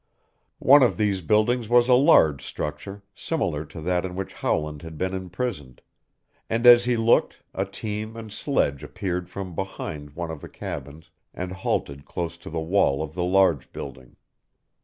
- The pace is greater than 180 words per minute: No, average, 170 wpm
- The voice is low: Yes, very low, 90 Hz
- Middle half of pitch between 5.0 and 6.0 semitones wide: Yes, wide, 5.6 semitones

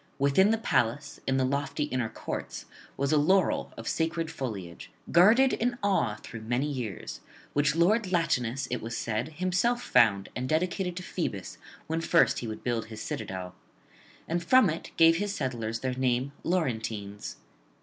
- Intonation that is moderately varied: No, wide, 7.0 semitones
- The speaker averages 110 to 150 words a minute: No, average, 160 wpm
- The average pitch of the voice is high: No, medium, 140 Hz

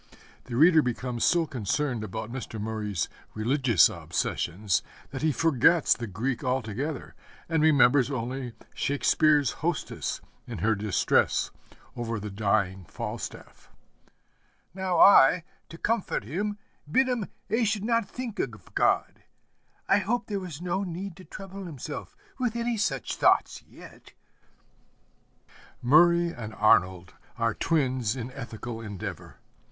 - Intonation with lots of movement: Yes, wide, 7.7 semitones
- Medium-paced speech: No, slow, 125 wpm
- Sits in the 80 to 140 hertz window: Yes, low, 135 Hz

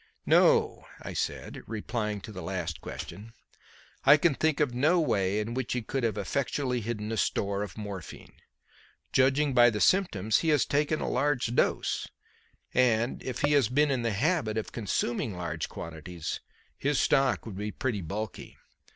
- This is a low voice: Yes, low, 115 Hz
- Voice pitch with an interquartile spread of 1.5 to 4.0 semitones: No, average, 5.0 semitones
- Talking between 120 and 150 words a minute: No, average, 170 wpm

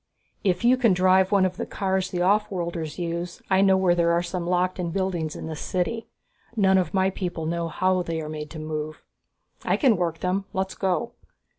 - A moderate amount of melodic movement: No, narrow, 2.1 semitones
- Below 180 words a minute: No, fast, 205 wpm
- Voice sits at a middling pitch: Yes, medium, 180 Hz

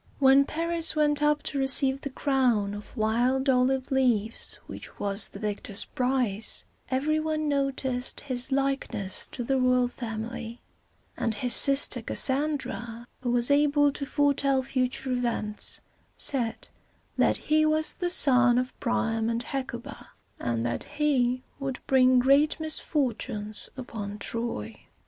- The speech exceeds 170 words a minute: No, slow, 135 wpm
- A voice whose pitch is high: Yes, very high, 255 Hz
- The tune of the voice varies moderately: Yes, average, 3.1 semitones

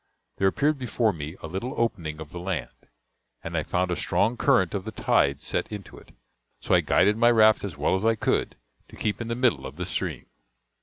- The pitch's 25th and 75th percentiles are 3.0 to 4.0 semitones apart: No, average, 5.1 semitones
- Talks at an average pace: No, fast, 220 wpm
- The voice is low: Yes, low, 100 Hz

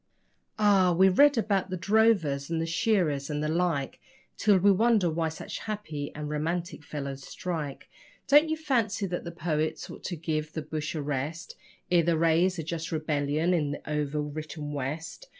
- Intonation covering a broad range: No, average, 3.9 semitones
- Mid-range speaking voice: Yes, medium, 165 Hz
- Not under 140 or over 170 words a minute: No, average, 180 wpm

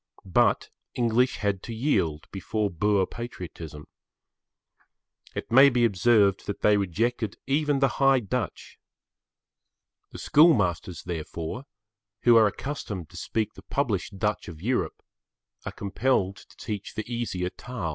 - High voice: No, low, 105 Hz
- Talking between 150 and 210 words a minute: No, slow, 135 wpm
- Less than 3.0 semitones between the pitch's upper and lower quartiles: No, average, 4.7 semitones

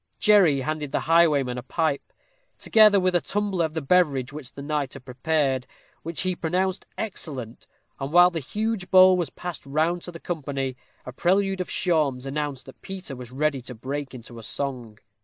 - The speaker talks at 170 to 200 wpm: Yes, average, 180 wpm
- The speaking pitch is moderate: Yes, medium, 155 Hz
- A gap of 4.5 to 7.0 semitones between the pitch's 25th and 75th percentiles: Yes, average, 4.9 semitones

